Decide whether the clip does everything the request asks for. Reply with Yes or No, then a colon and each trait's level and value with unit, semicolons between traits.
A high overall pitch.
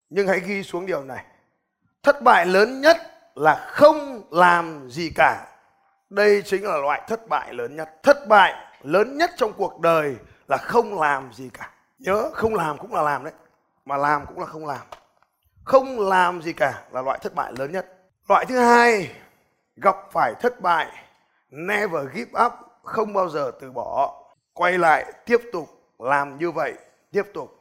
Yes: high, 200 Hz